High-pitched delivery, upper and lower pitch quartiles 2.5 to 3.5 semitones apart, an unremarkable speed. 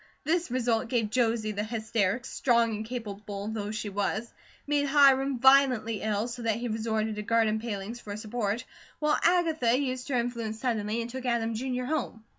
Yes: high, 230 Hz; average, 2.8 semitones; average, 180 wpm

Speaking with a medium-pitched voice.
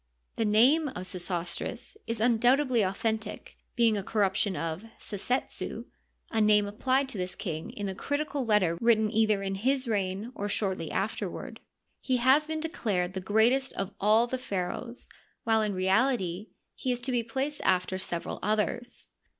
No: high, 215 Hz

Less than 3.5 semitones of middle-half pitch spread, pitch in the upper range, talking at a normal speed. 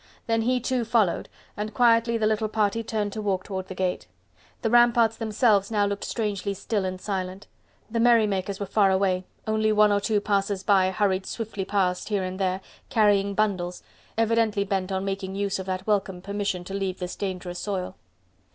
Yes: narrow, 2.4 semitones; high, 200 Hz; average, 185 wpm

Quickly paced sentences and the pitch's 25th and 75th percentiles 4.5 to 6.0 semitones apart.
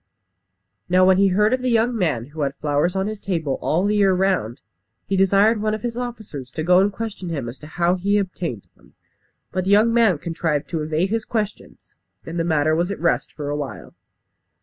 Yes: fast, 215 wpm; average, 5.0 semitones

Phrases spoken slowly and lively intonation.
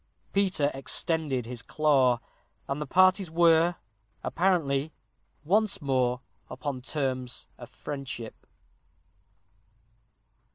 No: slow, 85 wpm; average, 4.6 semitones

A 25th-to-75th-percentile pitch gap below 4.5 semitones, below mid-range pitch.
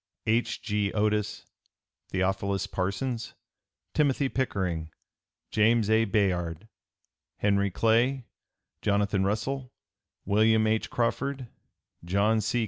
Yes: average, 2.9 semitones; low, 105 Hz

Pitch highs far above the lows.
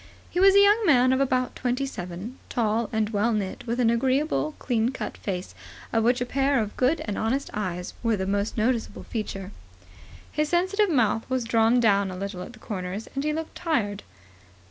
No: average, 4.7 semitones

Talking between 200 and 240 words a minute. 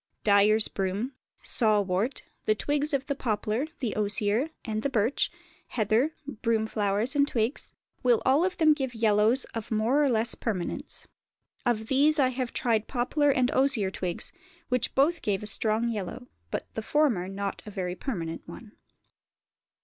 No: average, 160 wpm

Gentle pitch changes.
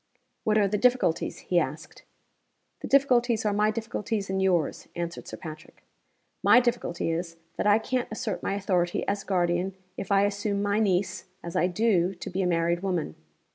No: average, 3.6 semitones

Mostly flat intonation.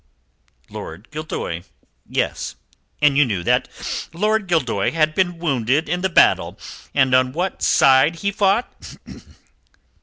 No: wide, 5.6 semitones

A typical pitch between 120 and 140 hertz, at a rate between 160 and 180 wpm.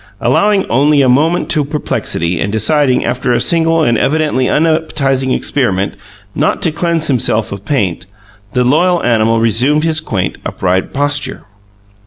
No: low, 135 Hz; average, 145 wpm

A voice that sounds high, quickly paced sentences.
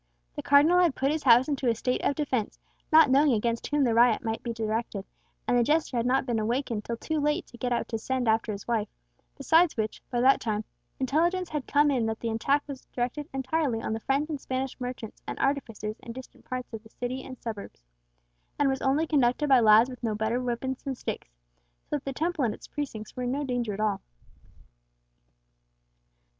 Yes: very high, 250 Hz; fast, 210 wpm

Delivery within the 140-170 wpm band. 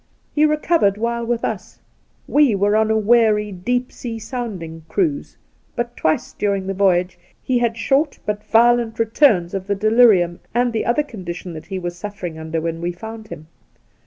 No: average, 185 wpm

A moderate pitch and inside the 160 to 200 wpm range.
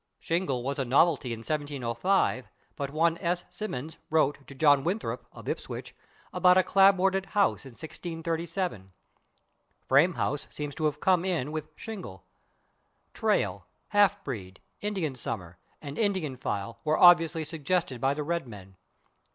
No: medium, 155 Hz; average, 145 wpm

